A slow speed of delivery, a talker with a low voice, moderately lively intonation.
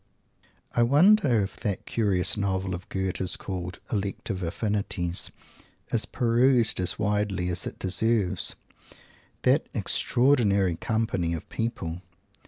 Yes: slow, 115 wpm; low, 100 Hz; average, 3.9 semitones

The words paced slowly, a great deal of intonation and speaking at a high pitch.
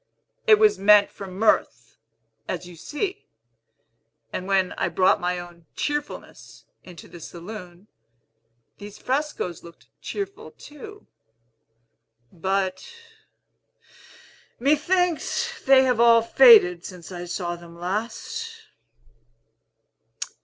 Yes: slow, 100 wpm; wide, 8.7 semitones; high, 200 Hz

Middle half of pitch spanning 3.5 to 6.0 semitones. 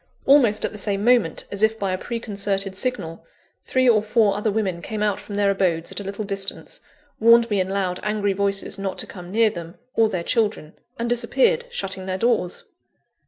No: average, 2.8 semitones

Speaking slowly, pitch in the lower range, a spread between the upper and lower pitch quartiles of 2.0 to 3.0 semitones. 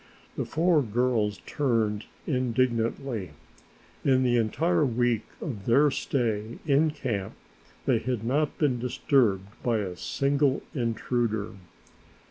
No: slow, 110 wpm; low, 120 Hz; average, 3.8 semitones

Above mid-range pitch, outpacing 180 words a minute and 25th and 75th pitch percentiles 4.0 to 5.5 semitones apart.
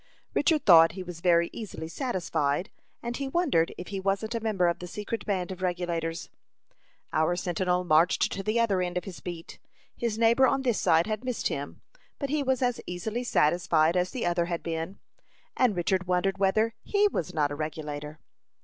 No: medium, 180 Hz; average, 190 wpm; average, 5.0 semitones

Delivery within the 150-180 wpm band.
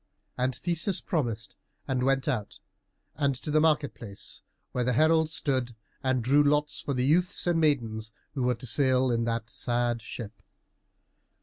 Yes: average, 165 wpm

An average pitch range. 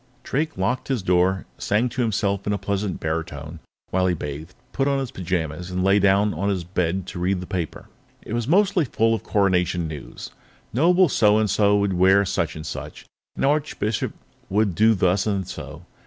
Yes: average, 3.6 semitones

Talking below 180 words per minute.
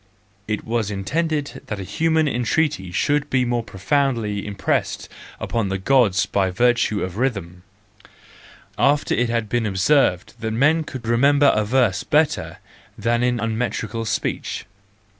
Yes: average, 140 wpm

